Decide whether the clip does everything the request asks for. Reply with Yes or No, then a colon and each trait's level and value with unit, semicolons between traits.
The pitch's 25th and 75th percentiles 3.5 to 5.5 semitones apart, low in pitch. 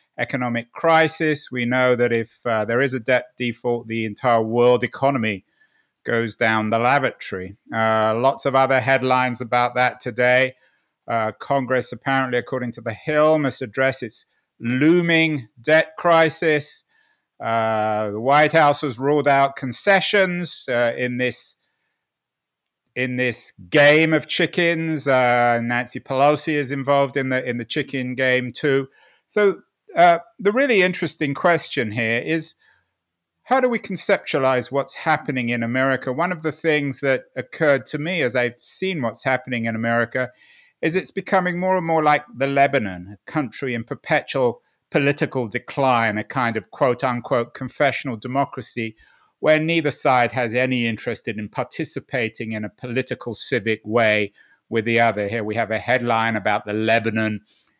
Yes: average, 4.2 semitones; low, 130 Hz